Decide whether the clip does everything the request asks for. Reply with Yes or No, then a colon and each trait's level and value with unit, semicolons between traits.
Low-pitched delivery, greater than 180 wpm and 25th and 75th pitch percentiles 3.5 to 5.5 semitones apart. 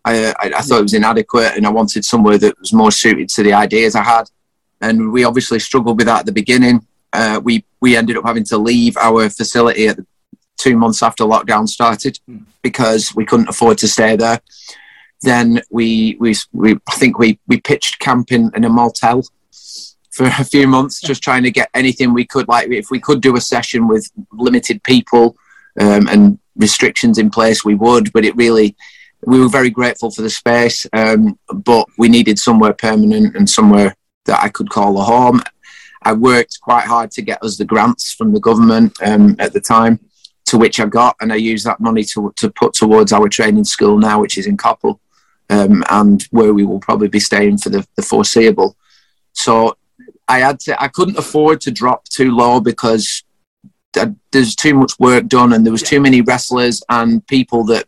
No: low, 120 Hz; average, 200 wpm; average, 2.7 semitones